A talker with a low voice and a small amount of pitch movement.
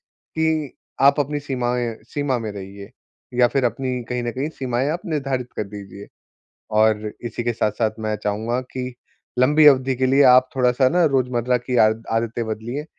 No: low, 125 Hz; average, 3.2 semitones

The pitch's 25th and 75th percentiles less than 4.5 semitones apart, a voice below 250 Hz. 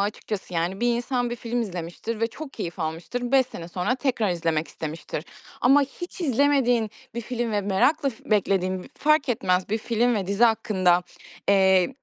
No: average, 4.9 semitones; high, 220 Hz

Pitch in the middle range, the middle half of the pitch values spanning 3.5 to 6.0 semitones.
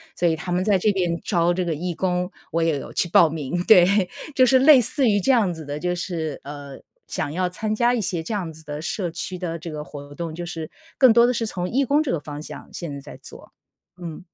Yes: medium, 175 Hz; average, 4.4 semitones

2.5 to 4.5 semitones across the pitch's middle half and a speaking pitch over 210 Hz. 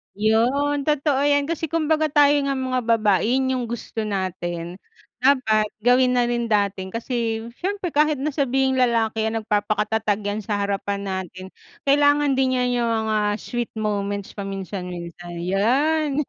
No: average, 5.3 semitones; high, 230 Hz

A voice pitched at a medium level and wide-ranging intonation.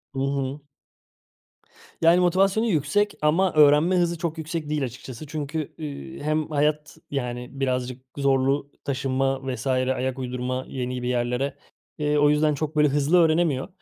No: medium, 145 Hz; average, 3.1 semitones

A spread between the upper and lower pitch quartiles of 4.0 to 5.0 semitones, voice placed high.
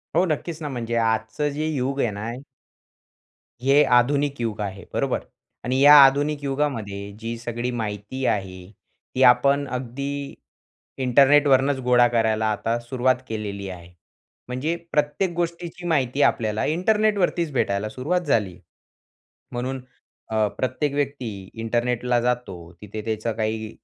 No: average, 4.3 semitones; low, 125 Hz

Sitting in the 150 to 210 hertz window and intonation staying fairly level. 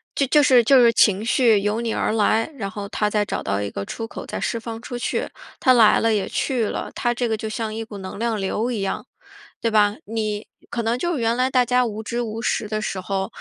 No: high, 225 Hz; narrow, 2.3 semitones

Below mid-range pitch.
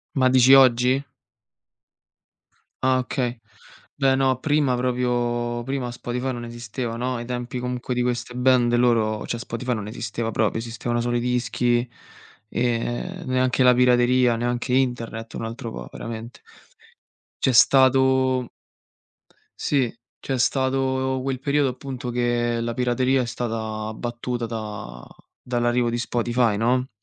Yes: low, 125 Hz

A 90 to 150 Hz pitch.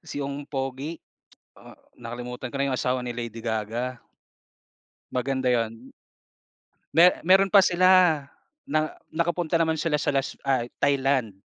Yes: low, 135 Hz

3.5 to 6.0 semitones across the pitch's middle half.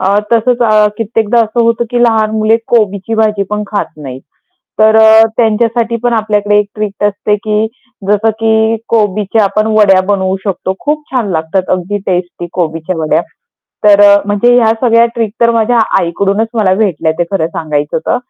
No: average, 2.7 semitones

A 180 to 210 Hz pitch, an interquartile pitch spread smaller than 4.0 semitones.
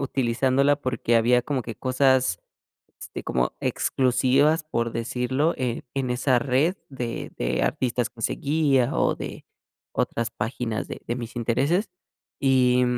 No: low, 125 Hz; narrow, 2.6 semitones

